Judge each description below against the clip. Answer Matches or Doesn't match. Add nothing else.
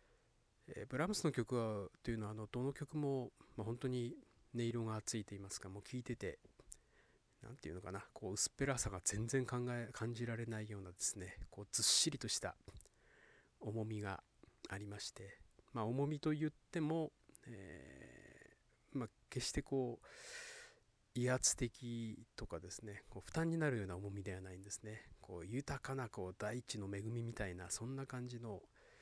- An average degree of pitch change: Matches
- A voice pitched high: Doesn't match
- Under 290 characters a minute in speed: Doesn't match